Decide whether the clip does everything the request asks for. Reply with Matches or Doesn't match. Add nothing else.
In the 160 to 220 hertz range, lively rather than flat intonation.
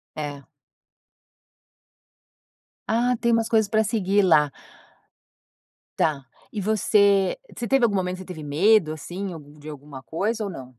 Matches